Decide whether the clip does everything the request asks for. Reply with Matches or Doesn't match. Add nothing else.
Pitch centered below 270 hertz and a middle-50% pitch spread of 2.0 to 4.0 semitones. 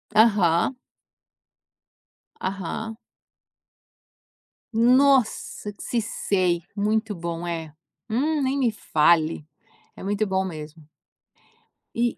Doesn't match